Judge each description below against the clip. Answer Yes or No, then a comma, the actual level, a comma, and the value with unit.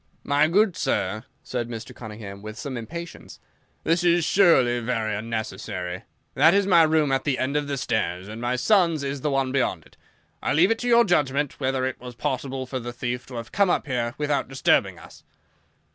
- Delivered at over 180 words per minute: Yes, average, 200 wpm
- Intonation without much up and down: No, average, 4.9 semitones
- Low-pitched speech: Yes, low, 130 Hz